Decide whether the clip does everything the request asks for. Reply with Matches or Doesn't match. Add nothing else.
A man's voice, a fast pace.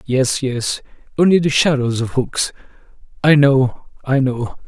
Doesn't match